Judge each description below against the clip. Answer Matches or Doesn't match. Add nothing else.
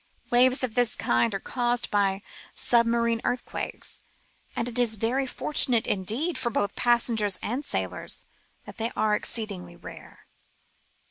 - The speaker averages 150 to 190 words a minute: Doesn't match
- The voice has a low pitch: Doesn't match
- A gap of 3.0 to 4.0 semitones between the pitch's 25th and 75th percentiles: Doesn't match